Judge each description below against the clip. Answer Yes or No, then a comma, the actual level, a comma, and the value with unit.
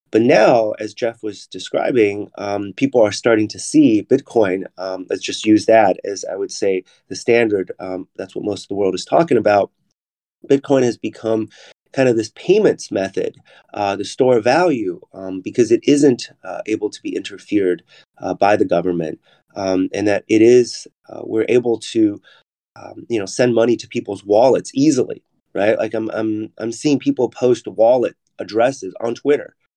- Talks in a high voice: No, low, 120 Hz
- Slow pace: No, average, 180 wpm